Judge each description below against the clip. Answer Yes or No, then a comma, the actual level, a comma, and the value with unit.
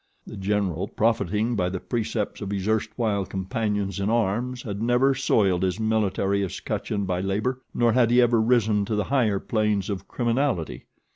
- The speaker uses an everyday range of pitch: Yes, average, 3.2 semitones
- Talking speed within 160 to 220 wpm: Yes, average, 165 wpm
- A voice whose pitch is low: Yes, low, 105 Hz